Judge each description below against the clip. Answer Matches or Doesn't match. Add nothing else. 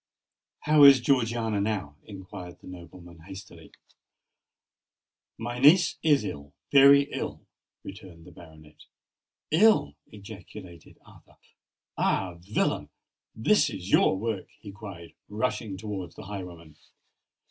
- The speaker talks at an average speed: Doesn't match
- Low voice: Matches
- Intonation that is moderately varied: Matches